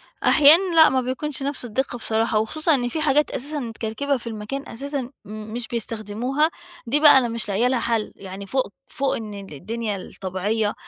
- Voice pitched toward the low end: No, high, 240 Hz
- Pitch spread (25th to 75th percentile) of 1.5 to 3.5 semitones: No, average, 4.4 semitones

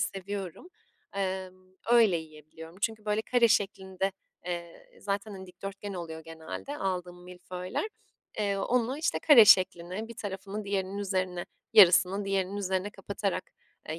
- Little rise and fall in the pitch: Yes, narrow, 2.1 semitones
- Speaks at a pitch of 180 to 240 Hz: Yes, high, 190 Hz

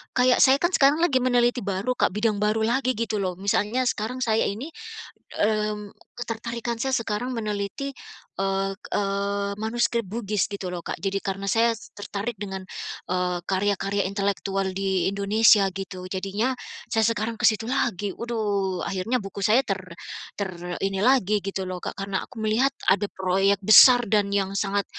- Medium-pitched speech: No, high, 205 Hz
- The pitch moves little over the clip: No, average, 3.0 semitones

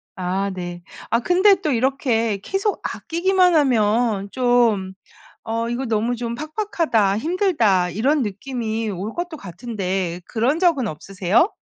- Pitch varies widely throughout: Yes, wide, 7.2 semitones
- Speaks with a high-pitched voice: Yes, high, 230 Hz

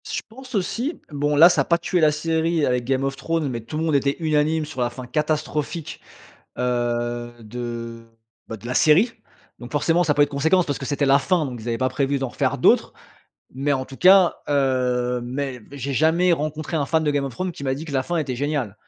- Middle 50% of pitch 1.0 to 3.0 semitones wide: No, average, 4.1 semitones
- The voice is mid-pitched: Yes, medium, 145 Hz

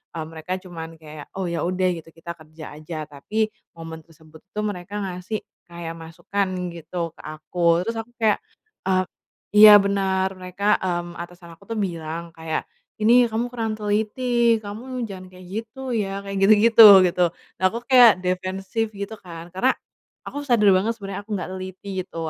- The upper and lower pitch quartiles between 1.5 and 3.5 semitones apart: No, average, 3.9 semitones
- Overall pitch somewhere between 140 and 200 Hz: Yes, high, 190 Hz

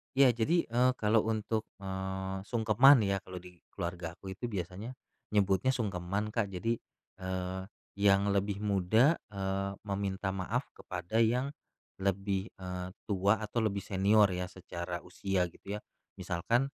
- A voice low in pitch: Yes, low, 100 Hz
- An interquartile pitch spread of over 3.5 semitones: No, average, 2.8 semitones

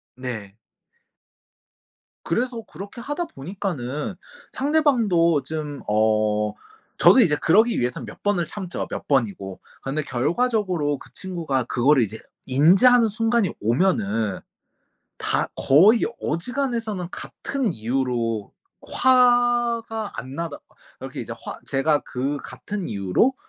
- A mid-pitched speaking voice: Yes, medium, 165 Hz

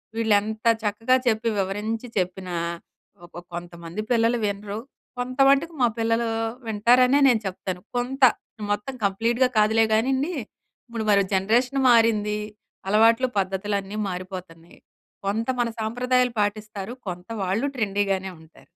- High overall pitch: Yes, high, 215 Hz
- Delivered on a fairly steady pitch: No, average, 3.5 semitones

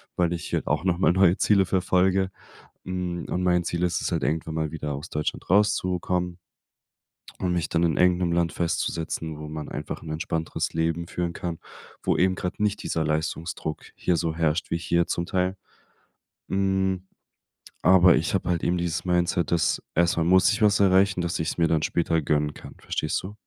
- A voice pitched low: Yes, very low, 85 Hz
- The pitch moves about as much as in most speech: No, narrow, 2.0 semitones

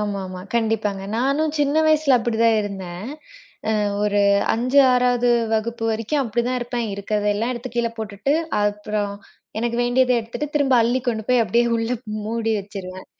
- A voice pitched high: Yes, high, 230 Hz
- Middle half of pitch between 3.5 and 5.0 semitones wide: No, average, 3.0 semitones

